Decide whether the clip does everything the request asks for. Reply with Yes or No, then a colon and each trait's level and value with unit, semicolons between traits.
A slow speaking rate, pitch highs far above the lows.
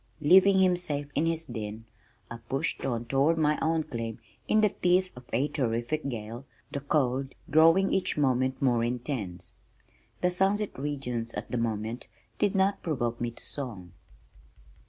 No: average, 155 wpm; wide, 5.8 semitones